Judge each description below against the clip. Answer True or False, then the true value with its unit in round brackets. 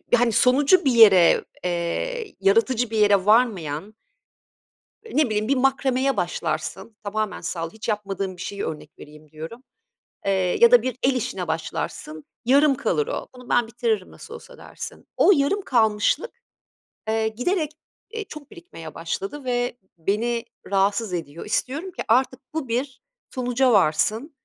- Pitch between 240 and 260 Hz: False (230 Hz)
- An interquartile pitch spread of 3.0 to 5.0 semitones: False (5.5 semitones)